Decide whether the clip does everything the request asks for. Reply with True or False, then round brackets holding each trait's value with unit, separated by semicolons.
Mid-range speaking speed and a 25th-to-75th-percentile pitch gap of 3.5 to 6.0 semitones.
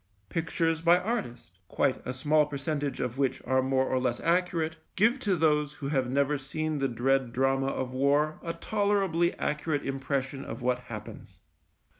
True (165 wpm; 3.8 semitones)